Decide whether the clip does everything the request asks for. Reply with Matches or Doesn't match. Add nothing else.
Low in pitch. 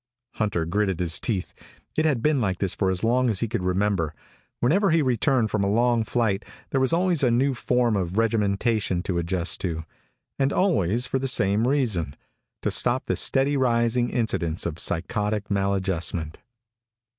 Matches